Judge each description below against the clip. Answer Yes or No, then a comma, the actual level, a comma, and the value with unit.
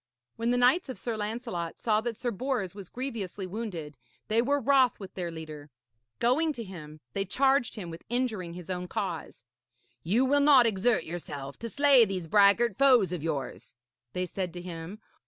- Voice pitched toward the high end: Yes, high, 205 Hz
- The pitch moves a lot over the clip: Yes, wide, 5.8 semitones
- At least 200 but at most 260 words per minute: No, average, 180 wpm